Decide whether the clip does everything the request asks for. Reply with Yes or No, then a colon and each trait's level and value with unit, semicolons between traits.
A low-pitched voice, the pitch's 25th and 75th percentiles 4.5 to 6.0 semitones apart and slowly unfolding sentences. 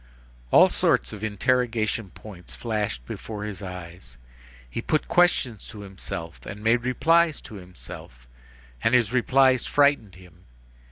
Yes: low, 110 Hz; average, 5.2 semitones; slow, 130 wpm